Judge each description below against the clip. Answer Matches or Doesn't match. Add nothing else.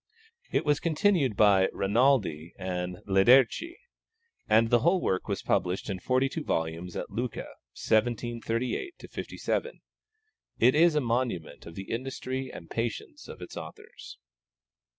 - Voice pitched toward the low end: Matches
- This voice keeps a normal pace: Doesn't match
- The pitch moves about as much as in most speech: Doesn't match